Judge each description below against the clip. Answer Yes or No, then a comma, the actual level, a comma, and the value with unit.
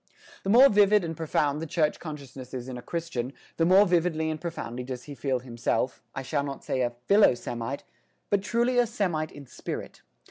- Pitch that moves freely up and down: Yes, wide, 5.7 semitones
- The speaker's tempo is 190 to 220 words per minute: Yes, average, 200 wpm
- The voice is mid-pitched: Yes, medium, 155 Hz